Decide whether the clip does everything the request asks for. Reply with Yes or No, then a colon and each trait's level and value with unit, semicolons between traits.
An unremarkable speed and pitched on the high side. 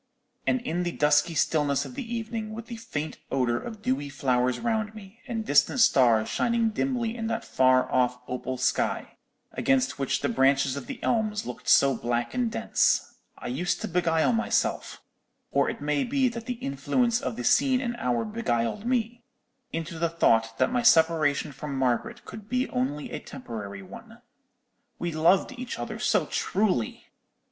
No: average, 170 wpm; medium, 175 Hz